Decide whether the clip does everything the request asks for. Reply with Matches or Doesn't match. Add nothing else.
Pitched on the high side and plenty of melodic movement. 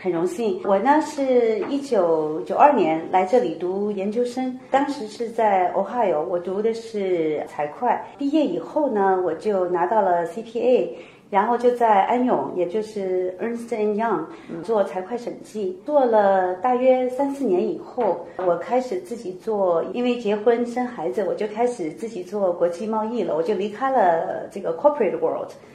Doesn't match